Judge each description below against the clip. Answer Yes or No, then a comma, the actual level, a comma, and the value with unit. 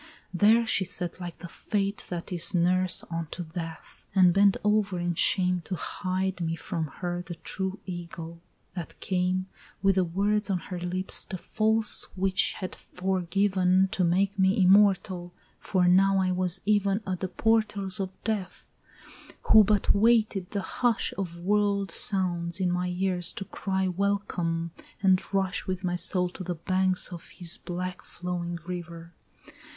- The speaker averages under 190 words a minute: Yes, average, 160 wpm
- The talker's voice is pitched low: No, medium, 185 Hz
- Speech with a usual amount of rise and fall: No, narrow, 1.9 semitones